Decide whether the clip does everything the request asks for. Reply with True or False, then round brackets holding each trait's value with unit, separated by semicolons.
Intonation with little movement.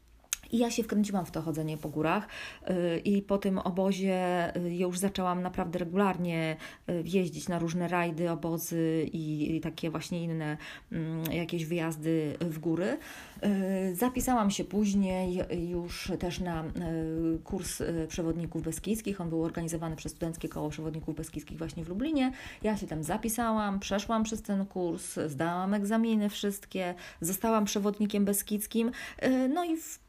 False (3.7 semitones)